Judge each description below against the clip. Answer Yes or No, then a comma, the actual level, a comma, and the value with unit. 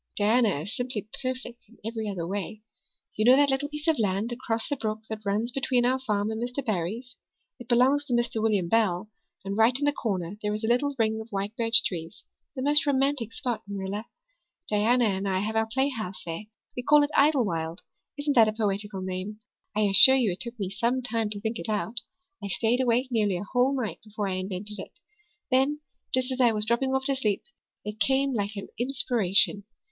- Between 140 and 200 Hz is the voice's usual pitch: No, high, 225 Hz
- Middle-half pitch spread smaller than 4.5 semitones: Yes, average, 3.9 semitones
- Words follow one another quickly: Yes, fast, 210 wpm